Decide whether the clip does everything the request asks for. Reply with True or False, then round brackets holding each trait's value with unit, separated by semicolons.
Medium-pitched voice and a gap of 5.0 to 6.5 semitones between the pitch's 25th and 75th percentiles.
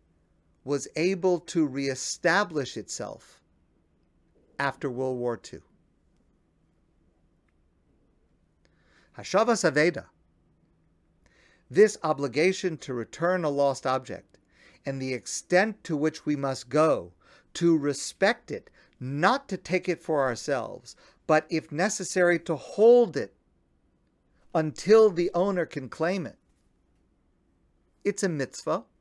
True (155 Hz; 5.3 semitones)